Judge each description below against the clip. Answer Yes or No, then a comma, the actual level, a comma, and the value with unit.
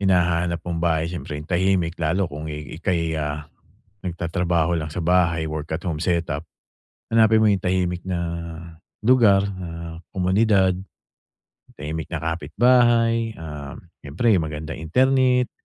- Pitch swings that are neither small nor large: Yes, average, 3.5 semitones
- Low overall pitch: Yes, very low, 85 Hz